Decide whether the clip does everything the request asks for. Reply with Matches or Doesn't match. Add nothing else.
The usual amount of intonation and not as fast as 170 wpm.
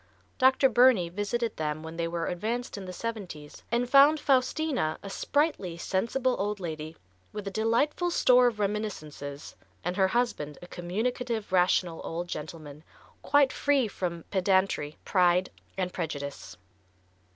Doesn't match